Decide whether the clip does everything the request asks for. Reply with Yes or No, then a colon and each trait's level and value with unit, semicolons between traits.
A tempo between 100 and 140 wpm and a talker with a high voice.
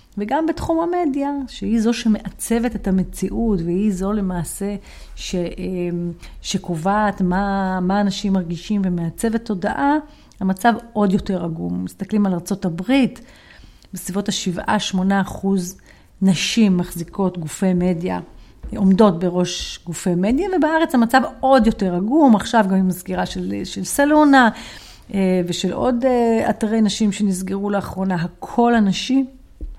Yes: average, 115 wpm; high, 200 Hz